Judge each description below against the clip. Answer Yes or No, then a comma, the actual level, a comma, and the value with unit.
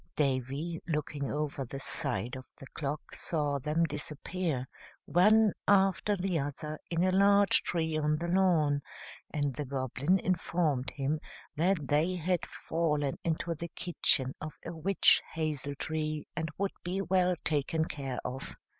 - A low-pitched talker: No, medium, 155 Hz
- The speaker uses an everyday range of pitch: Yes, average, 3.7 semitones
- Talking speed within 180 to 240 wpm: No, average, 145 wpm